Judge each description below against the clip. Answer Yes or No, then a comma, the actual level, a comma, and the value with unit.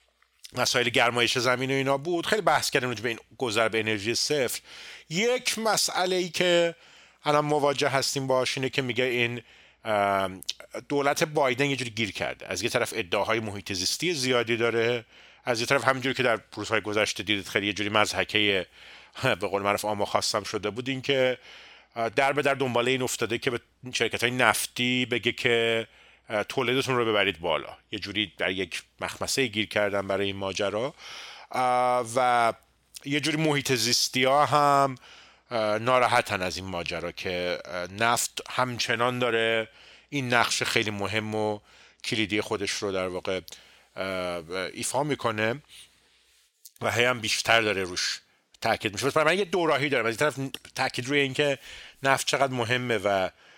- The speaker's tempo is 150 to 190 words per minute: Yes, fast, 155 wpm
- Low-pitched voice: Yes, low, 120 Hz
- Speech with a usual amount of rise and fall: Yes, average, 4.1 semitones